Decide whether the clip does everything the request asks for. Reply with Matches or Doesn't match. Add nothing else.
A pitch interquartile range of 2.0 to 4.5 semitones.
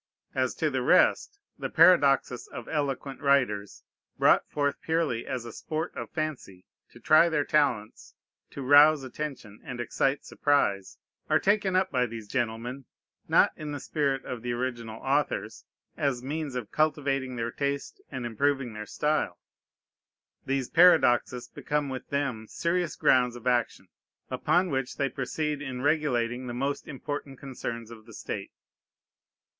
Matches